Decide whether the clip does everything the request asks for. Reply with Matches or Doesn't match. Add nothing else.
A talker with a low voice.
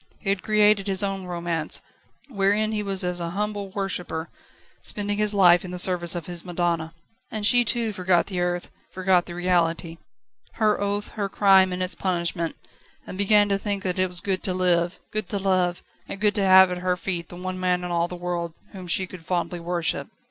Doesn't match